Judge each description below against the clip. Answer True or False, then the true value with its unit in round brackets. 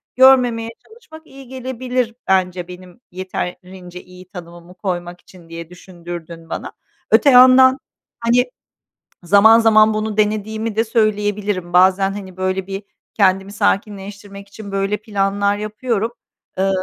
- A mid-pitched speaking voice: False (200 Hz)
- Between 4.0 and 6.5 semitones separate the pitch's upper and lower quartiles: False (3.4 semitones)